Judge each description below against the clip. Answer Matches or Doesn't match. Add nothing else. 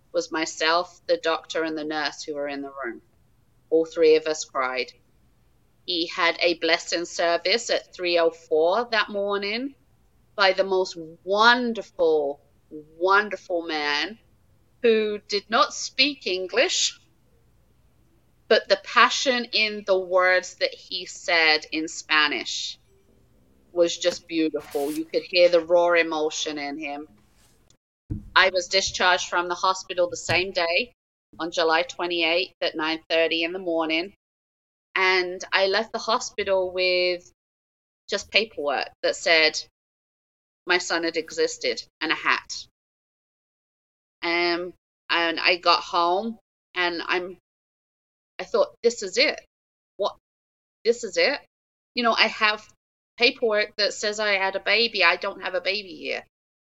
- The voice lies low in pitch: Doesn't match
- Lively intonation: Doesn't match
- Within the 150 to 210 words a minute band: Doesn't match